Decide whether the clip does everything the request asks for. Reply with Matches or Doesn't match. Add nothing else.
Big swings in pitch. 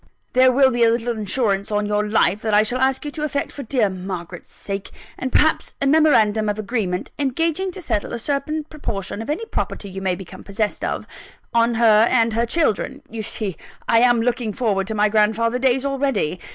Doesn't match